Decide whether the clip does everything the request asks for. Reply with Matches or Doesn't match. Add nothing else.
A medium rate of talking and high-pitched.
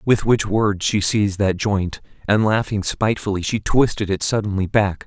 Doesn't match